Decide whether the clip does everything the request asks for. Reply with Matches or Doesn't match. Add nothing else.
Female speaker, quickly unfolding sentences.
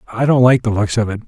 Doesn't match